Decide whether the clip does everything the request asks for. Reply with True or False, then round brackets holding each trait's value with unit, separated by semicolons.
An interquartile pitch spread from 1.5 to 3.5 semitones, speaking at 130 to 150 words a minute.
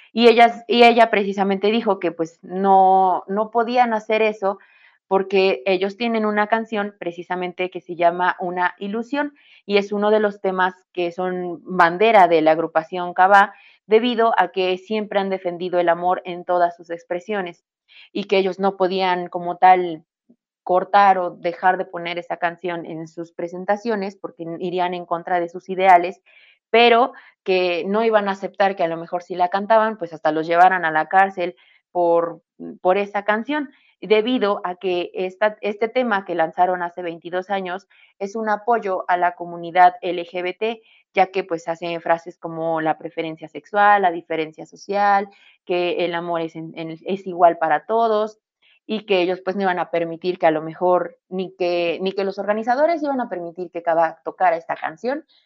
False (3.0 semitones; 175 wpm)